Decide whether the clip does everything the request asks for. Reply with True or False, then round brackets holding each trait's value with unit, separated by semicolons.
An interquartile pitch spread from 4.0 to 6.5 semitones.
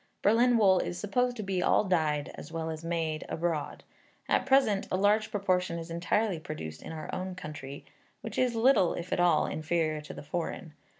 True (4.5 semitones)